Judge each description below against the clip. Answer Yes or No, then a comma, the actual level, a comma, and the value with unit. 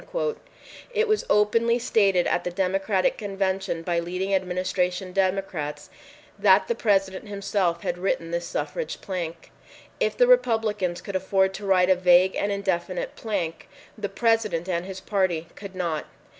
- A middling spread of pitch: No, narrow, 2.3 semitones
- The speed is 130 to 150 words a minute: Yes, average, 145 wpm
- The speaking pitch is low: No, high, 190 Hz